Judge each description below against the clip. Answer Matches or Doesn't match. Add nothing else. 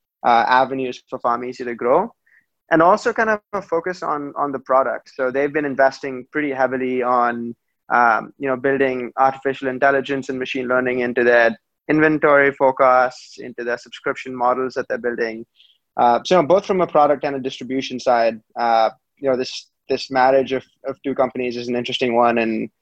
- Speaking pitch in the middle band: Doesn't match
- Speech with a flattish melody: Matches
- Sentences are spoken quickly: Doesn't match